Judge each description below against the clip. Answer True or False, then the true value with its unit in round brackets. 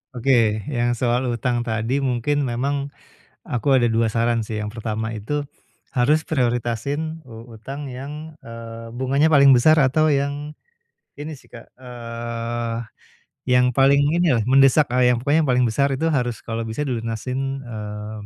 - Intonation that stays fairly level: False (3.2 semitones)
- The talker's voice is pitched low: True (125 Hz)